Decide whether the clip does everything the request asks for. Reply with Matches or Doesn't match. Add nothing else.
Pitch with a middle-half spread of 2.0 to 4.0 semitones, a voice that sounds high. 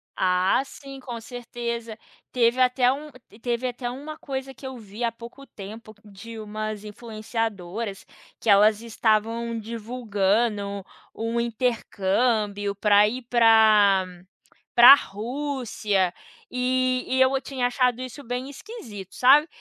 Matches